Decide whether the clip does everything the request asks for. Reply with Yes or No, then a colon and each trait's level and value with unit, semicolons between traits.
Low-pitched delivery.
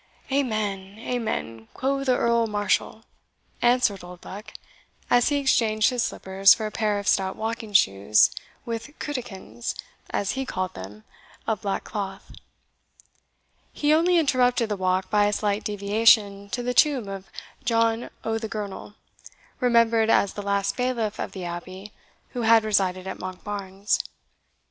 No: high, 210 Hz